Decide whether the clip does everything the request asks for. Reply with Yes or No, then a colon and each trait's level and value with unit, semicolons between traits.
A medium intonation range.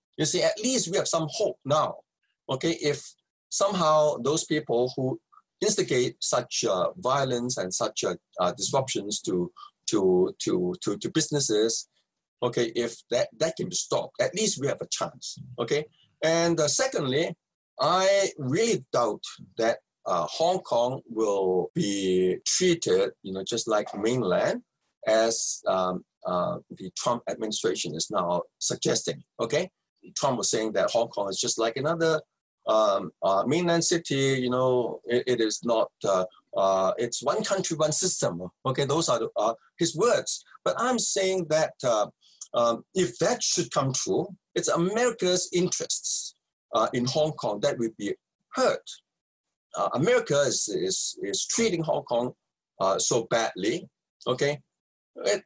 No: wide, 7.6 semitones